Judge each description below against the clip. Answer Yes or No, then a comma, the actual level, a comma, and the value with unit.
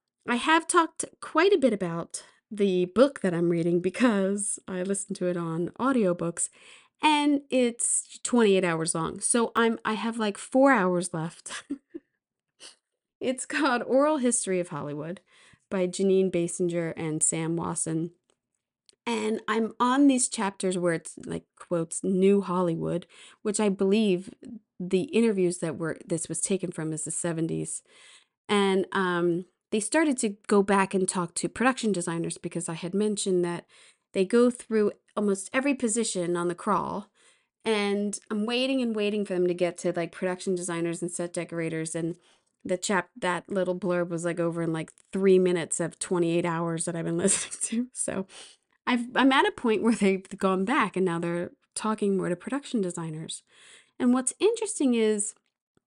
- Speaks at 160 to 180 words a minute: Yes, average, 165 wpm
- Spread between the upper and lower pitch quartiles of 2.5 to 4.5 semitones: No, average, 5.0 semitones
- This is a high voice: Yes, high, 195 Hz